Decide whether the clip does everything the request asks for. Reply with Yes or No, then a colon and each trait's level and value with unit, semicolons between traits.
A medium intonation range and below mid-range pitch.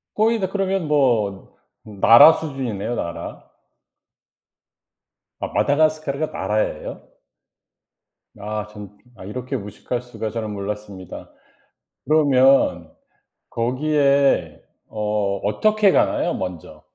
No: wide, 6.3 semitones; low, 120 Hz